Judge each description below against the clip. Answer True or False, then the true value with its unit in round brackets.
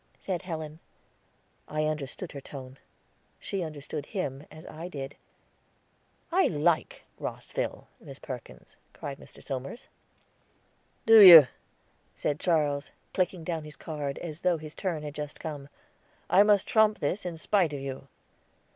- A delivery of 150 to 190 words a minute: False (140 wpm)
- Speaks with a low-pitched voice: False (155 Hz)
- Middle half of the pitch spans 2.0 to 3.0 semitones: False (3.6 semitones)